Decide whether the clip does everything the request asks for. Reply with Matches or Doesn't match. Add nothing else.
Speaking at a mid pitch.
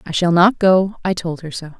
Matches